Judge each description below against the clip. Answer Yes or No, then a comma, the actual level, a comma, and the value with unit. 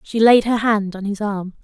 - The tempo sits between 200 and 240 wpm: No, fast, 255 wpm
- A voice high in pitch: Yes, high, 210 Hz